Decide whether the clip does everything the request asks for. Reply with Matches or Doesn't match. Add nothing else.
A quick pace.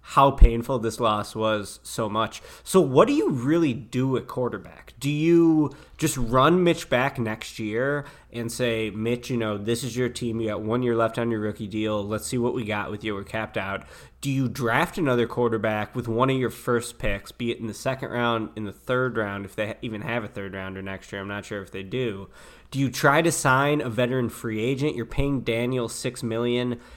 Matches